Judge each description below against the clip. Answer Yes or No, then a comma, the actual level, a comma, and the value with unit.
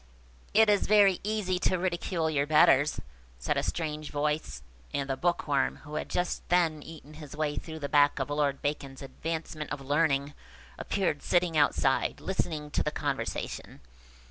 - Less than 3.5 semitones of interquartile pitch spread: Yes, average, 3.1 semitones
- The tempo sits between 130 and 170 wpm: Yes, average, 160 wpm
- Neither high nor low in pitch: Yes, medium, 150 Hz